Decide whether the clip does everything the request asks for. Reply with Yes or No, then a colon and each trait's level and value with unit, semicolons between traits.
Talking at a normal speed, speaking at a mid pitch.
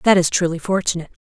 Yes: average, 195 wpm; medium, 175 Hz